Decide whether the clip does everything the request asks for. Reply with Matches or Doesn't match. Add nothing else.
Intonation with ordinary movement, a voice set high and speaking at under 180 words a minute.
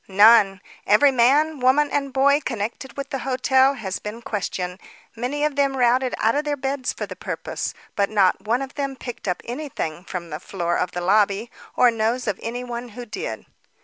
Doesn't match